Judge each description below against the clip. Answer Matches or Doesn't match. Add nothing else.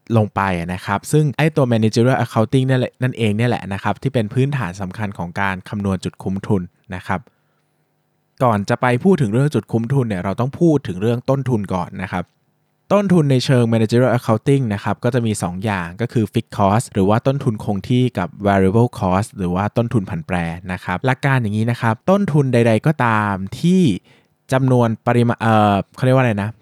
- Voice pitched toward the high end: Doesn't match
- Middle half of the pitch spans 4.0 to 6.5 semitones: Matches